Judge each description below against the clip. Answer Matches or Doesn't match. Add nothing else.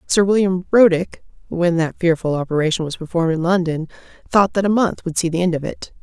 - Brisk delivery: Matches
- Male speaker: Doesn't match